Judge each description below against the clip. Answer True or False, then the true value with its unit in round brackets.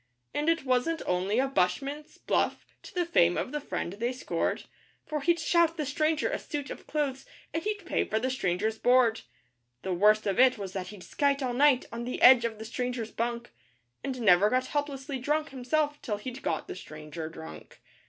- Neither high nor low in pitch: False (255 Hz)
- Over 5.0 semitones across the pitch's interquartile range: True (5.5 semitones)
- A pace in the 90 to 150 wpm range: False (200 wpm)